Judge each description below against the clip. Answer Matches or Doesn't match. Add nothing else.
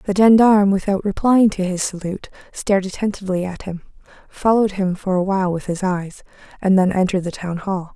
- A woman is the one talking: Matches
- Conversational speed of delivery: Matches